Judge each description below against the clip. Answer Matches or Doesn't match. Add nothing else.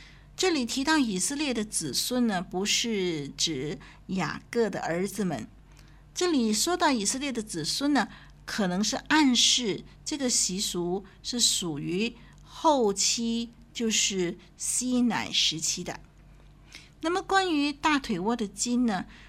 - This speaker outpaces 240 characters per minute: Doesn't match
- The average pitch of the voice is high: Matches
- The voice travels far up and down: Matches